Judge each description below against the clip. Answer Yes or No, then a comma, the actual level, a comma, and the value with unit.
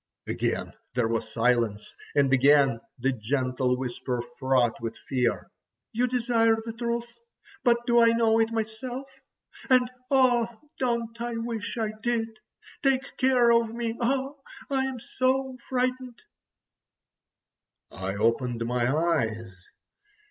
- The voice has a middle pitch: No, high, 225 Hz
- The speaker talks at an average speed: No, slow, 120 wpm